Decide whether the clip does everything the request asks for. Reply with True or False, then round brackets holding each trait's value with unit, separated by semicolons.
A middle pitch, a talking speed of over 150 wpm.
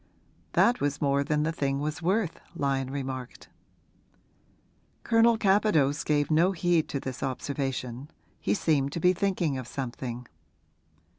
False (145 Hz; 135 wpm)